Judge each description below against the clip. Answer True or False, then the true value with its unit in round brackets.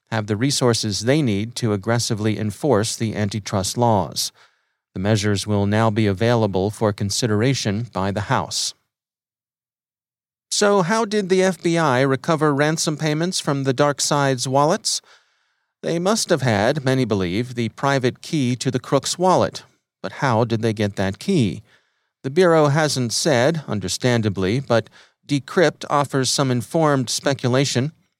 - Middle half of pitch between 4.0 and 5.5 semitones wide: True (5.0 semitones)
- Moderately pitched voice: False (125 Hz)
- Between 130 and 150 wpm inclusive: True (140 wpm)